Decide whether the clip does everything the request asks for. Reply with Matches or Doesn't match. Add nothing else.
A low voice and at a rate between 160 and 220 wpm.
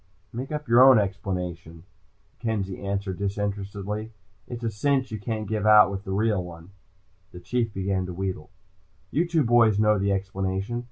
Matches